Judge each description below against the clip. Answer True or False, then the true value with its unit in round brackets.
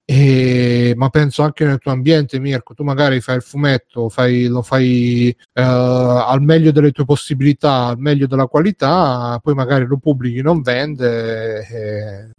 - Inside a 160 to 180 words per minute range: False (145 wpm)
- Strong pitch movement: False (2.9 semitones)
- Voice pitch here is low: True (130 Hz)